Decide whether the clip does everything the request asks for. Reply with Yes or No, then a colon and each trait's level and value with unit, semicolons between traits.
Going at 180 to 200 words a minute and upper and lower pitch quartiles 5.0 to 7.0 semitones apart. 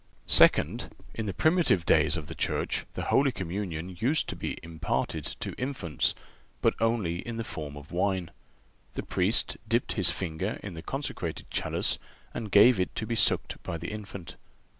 No: average, 165 wpm; average, 5.3 semitones